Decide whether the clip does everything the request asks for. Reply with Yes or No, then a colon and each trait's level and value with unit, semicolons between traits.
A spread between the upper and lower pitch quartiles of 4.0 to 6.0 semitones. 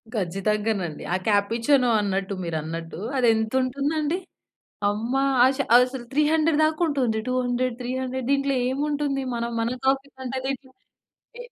Yes: average, 4.3 semitones